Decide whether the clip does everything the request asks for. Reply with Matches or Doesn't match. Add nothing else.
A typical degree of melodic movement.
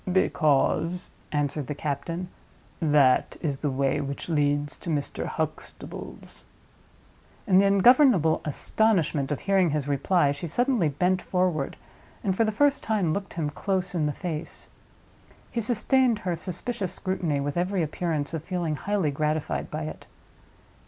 Matches